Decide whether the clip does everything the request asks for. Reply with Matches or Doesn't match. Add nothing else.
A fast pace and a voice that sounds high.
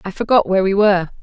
Matches